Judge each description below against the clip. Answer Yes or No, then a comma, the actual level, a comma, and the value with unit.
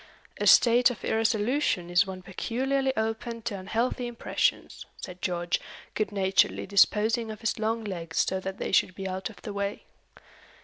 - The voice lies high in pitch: Yes, high, 210 Hz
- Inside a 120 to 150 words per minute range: No, average, 165 wpm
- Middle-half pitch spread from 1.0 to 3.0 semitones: No, average, 3.4 semitones